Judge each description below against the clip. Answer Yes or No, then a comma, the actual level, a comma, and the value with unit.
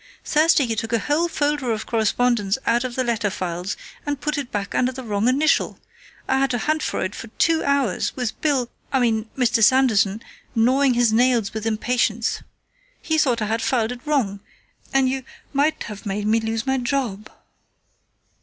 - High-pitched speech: Yes, high, 240 Hz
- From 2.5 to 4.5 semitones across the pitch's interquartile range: Yes, average, 3.6 semitones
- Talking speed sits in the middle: Yes, average, 185 wpm